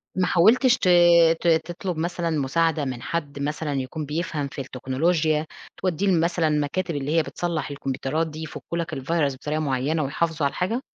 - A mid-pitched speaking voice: Yes, medium, 155 Hz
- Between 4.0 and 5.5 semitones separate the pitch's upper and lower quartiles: No, average, 3.0 semitones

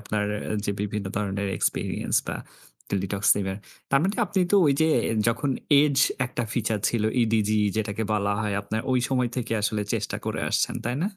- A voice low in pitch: Yes, low, 110 Hz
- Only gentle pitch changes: No, average, 3.6 semitones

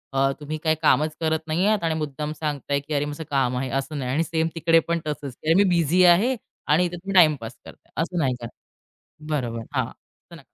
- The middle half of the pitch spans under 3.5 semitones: Yes, average, 2.9 semitones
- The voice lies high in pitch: No, medium, 155 Hz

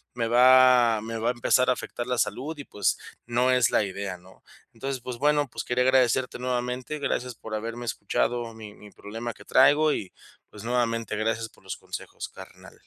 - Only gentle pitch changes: Yes, narrow, 2.3 semitones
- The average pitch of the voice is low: Yes, low, 120 Hz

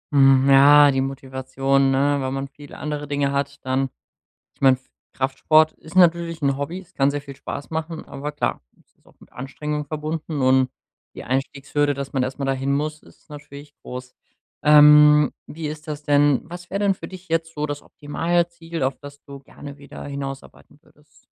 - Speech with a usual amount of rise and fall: No, narrow, 2.0 semitones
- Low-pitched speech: No, medium, 145 Hz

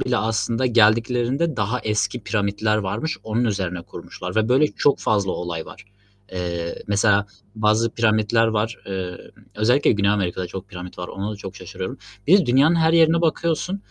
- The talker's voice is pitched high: No, low, 110 Hz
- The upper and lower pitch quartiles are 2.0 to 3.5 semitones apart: No, average, 4.1 semitones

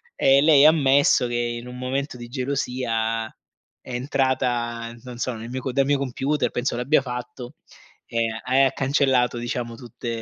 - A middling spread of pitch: No, narrow, 2.2 semitones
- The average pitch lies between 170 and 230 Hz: No, low, 125 Hz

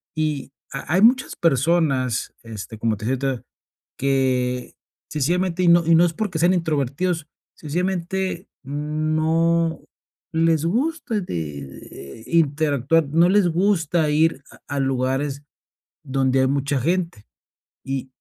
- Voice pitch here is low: No, medium, 155 Hz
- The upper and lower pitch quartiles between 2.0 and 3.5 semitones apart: No, average, 4.2 semitones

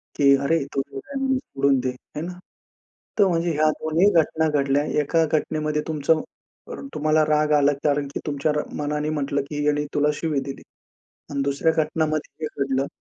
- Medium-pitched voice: Yes, medium, 150 Hz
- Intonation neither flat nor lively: No, narrow, 1.9 semitones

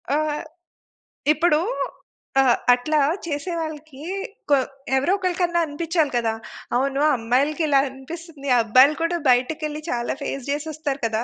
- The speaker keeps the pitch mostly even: No, average, 3.3 semitones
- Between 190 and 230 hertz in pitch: No, very high, 290 Hz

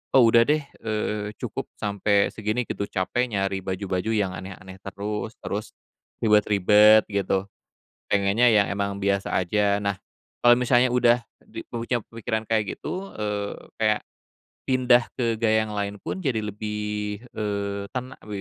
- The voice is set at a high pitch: No, low, 105 Hz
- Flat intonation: Yes, narrow, 2.2 semitones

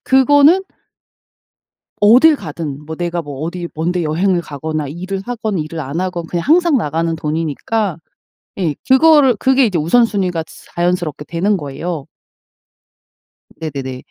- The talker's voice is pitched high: No, medium, 175 Hz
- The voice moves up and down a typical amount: No, wide, 5.7 semitones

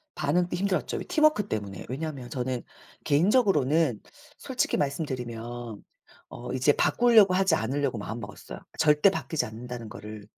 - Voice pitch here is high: No, medium, 140 Hz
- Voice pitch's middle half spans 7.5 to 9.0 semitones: No, wide, 6.8 semitones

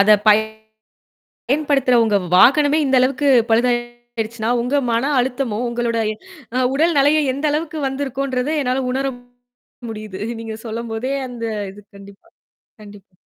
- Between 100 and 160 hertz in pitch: No, high, 245 Hz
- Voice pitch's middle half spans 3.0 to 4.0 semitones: Yes, average, 3.6 semitones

